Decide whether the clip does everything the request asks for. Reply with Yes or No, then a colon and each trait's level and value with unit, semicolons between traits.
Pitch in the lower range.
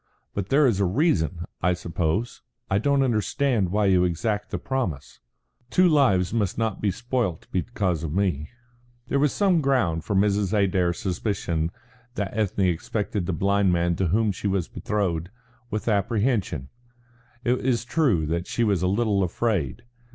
Yes: low, 100 Hz